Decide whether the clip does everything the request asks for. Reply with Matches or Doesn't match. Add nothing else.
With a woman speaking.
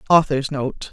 Matches